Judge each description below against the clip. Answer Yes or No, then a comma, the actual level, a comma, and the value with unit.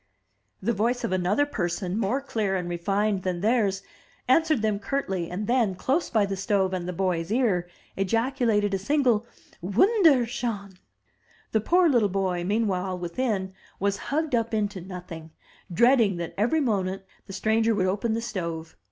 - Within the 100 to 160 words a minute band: Yes, average, 155 wpm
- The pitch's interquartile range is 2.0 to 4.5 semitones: Yes, average, 4.1 semitones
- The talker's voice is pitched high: Yes, high, 205 Hz